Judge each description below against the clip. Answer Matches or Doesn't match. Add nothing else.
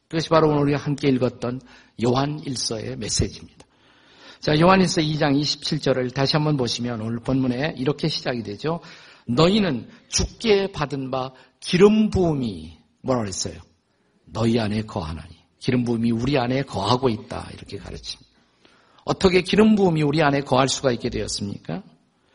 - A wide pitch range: Doesn't match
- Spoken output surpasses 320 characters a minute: Matches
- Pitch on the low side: Matches